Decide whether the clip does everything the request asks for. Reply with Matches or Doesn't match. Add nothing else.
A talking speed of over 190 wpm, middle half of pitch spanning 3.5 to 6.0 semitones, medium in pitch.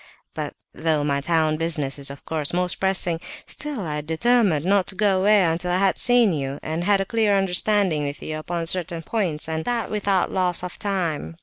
Matches